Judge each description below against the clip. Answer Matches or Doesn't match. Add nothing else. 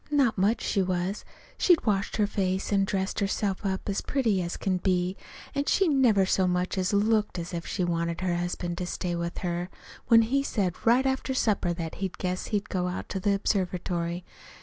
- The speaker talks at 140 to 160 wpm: Doesn't match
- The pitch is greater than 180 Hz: Matches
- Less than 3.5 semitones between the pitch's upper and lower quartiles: Matches